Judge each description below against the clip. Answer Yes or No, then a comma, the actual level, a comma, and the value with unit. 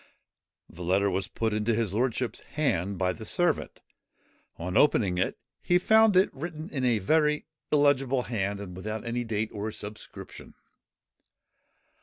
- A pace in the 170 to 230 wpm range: No, average, 140 wpm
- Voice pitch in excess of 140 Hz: No, low, 110 Hz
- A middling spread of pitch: No, wide, 6.3 semitones